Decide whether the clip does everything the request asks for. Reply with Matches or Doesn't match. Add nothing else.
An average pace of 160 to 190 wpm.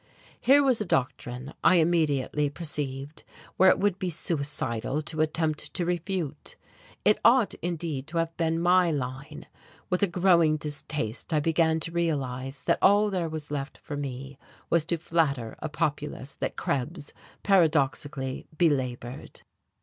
Doesn't match